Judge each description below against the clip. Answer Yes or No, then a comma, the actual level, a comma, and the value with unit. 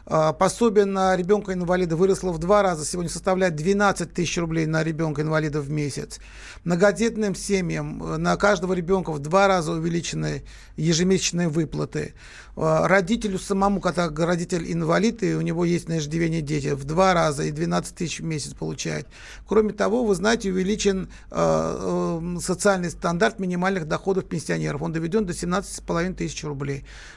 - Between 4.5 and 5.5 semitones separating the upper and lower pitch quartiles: No, average, 3.3 semitones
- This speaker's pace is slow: No, average, 145 wpm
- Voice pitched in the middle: Yes, medium, 175 Hz